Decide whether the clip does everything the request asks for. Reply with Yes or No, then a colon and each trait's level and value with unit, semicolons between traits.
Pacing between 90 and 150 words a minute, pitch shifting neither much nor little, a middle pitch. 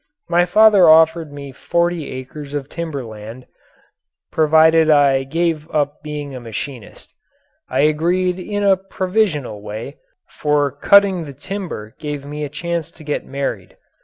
Yes: average, 140 wpm; average, 3.6 semitones; medium, 150 Hz